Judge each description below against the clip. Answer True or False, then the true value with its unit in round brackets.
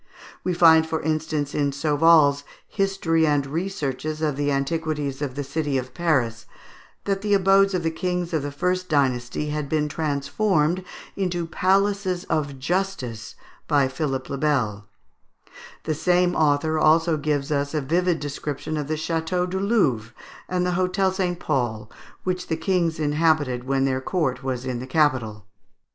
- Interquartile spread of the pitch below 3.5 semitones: False (4.2 semitones)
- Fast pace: False (155 wpm)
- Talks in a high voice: False (155 Hz)